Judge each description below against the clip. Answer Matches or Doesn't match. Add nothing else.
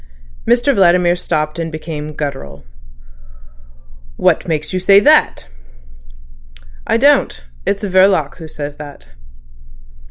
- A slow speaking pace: Matches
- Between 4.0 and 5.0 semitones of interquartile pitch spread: Matches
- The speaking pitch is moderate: Matches